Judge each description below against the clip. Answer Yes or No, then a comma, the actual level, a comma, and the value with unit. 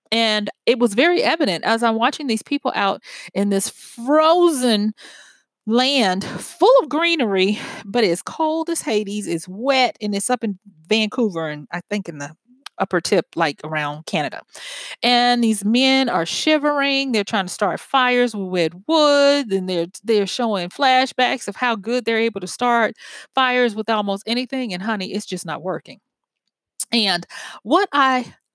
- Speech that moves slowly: No, average, 160 wpm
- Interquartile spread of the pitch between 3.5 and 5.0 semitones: Yes, average, 4.6 semitones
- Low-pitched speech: No, high, 230 Hz